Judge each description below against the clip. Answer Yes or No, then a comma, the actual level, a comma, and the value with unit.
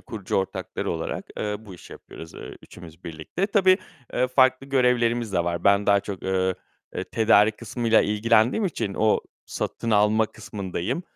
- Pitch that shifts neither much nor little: Yes, average, 4.0 semitones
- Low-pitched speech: Yes, low, 110 Hz